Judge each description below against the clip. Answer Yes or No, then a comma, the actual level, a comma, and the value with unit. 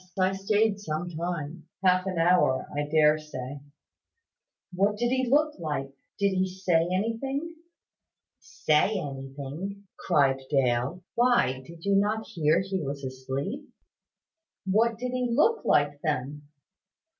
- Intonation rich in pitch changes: Yes, wide, 6.1 semitones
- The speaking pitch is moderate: Yes, medium, 180 Hz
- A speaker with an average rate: No, slow, 130 wpm